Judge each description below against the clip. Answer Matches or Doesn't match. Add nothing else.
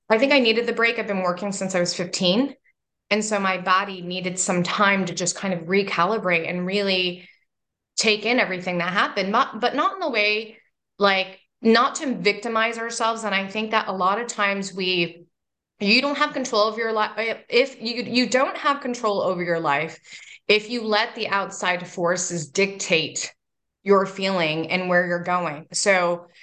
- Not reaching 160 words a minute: Doesn't match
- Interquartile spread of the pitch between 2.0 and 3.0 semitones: Doesn't match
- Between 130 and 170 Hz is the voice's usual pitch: Doesn't match